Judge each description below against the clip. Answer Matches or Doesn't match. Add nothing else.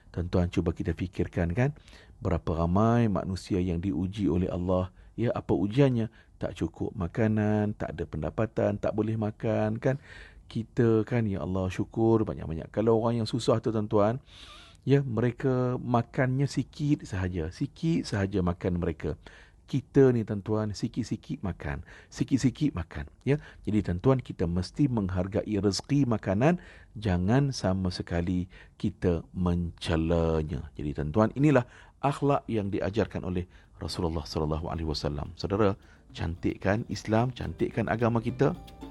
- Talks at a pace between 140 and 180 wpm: Doesn't match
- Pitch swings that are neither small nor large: Matches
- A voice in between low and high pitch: Doesn't match